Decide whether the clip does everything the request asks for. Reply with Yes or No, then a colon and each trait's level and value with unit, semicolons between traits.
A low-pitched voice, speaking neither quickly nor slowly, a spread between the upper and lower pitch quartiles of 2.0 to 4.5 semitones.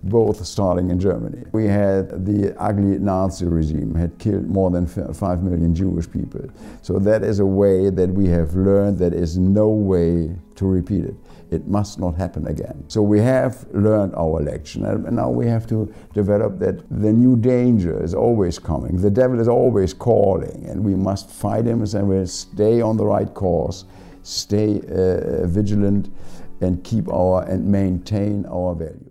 Yes: very low, 95 Hz; average, 175 wpm; average, 2.7 semitones